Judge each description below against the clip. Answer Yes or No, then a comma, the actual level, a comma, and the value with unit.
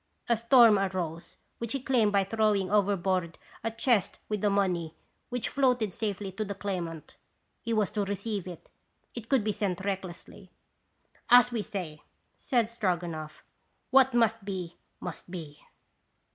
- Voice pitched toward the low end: No, high, 200 Hz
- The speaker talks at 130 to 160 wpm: Yes, average, 145 wpm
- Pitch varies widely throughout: No, average, 3.7 semitones